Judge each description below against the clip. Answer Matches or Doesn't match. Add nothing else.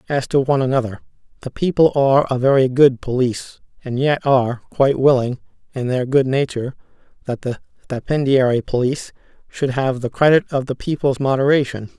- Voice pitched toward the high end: Doesn't match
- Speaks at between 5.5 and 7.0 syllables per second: Matches